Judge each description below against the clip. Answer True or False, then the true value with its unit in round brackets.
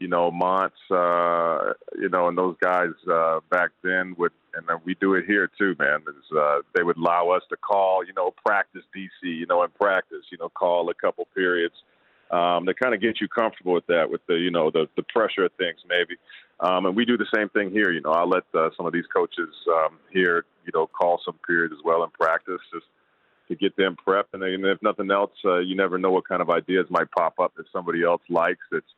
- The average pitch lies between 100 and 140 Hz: False (90 Hz)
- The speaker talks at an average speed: False (240 wpm)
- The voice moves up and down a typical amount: False (1.8 semitones)